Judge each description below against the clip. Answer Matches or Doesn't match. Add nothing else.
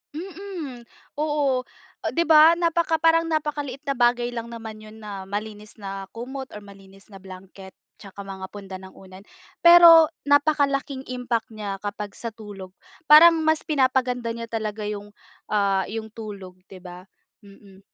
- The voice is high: Matches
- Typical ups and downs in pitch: Doesn't match